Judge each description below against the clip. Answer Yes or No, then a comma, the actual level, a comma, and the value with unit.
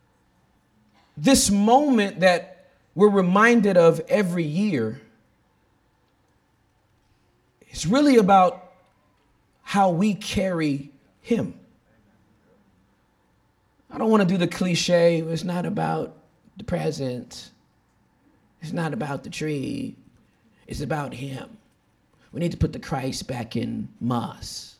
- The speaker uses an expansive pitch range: Yes, wide, 7.8 semitones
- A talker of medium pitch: Yes, medium, 170 Hz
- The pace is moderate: No, slow, 105 wpm